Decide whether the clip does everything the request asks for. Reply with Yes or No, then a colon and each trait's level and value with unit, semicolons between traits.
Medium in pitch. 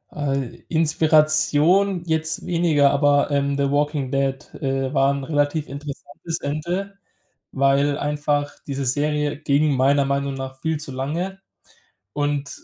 Yes: medium, 145 Hz